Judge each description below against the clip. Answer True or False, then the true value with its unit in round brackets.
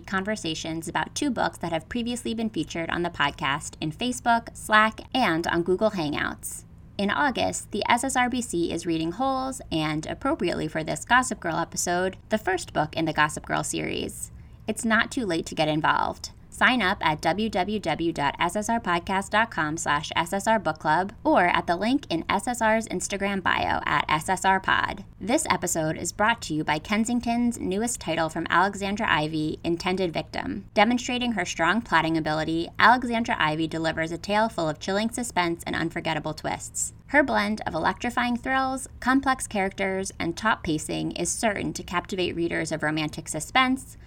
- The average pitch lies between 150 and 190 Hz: True (185 Hz)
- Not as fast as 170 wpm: True (155 wpm)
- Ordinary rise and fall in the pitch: False (5.9 semitones)